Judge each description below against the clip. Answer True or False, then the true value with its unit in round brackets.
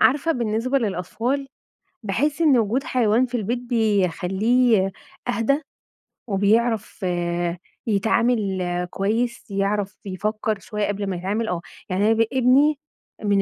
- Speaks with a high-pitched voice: True (220 Hz)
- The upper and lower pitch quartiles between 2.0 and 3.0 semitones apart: False (3.6 semitones)